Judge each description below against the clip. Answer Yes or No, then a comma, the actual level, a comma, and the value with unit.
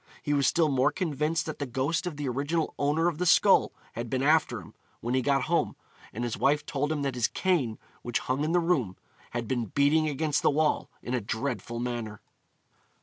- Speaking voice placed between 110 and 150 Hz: Yes, medium, 140 Hz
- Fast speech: Yes, fast, 210 wpm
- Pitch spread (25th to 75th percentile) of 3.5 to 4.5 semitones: Yes, average, 4.2 semitones